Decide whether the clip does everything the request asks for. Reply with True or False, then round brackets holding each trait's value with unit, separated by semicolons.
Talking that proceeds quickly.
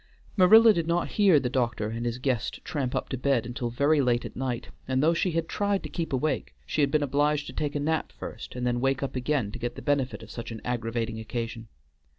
True (240 wpm)